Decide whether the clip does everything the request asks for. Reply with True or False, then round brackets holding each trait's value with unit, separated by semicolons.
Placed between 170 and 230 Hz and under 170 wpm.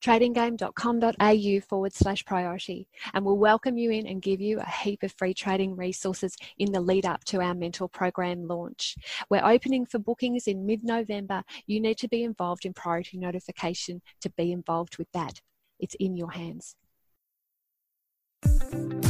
True (190 Hz; 160 wpm)